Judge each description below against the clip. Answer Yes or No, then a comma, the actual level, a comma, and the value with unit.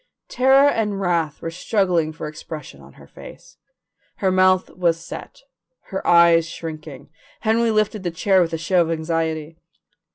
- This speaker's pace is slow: No, average, 155 wpm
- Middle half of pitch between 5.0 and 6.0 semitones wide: No, average, 3.3 semitones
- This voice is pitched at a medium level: Yes, medium, 170 Hz